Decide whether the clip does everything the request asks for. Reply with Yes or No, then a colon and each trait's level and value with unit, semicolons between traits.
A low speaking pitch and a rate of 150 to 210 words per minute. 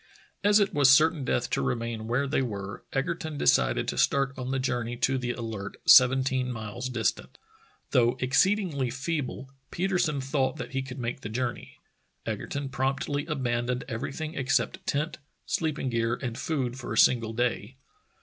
Yes: low, 130 Hz; average, 160 wpm